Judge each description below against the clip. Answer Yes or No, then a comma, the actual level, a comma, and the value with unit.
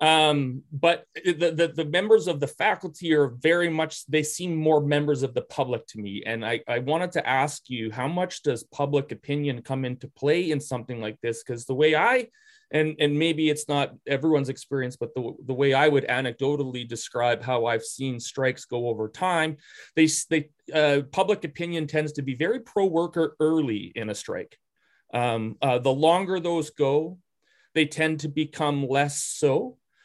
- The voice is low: No, medium, 150 Hz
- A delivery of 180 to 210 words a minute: Yes, average, 185 wpm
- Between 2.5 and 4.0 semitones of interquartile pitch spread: Yes, average, 3.6 semitones